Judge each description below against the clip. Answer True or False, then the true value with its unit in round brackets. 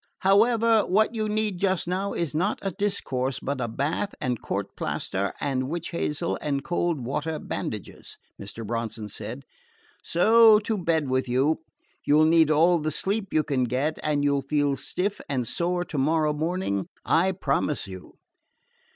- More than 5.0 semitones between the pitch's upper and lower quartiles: True (5.5 semitones)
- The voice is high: False (155 Hz)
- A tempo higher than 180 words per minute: False (170 wpm)